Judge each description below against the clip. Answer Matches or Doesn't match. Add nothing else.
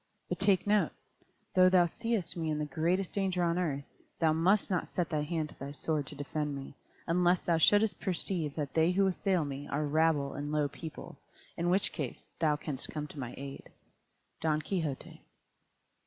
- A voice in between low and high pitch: Matches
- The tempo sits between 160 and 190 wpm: Matches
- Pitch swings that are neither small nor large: Matches